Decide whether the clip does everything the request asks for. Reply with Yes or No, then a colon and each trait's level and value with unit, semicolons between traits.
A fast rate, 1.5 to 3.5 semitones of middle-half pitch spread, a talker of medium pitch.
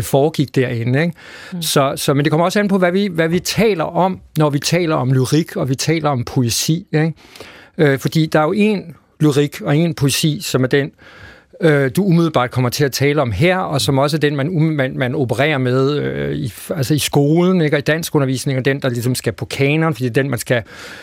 Yes: fast, 235 wpm; average, 3.2 semitones; medium, 145 Hz